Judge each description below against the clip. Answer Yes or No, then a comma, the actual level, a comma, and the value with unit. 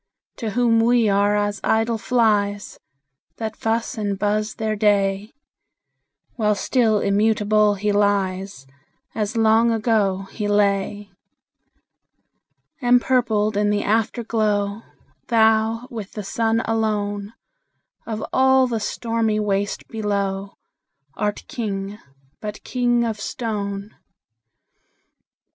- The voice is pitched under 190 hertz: No, high, 215 Hz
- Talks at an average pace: No, slow, 105 wpm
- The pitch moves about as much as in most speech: No, narrow, 1.9 semitones